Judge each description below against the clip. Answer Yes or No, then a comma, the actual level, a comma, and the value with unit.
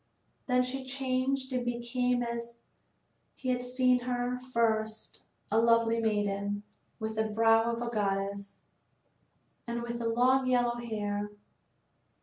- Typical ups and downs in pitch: No, narrow, 2.3 semitones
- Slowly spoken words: Yes, slow, 125 wpm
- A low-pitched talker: No, high, 235 Hz